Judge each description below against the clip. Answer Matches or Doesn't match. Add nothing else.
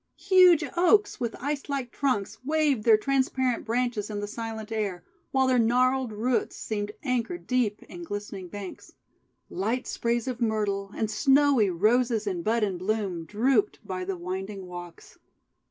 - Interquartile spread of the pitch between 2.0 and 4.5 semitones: Matches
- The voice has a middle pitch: Doesn't match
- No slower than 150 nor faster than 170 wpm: Matches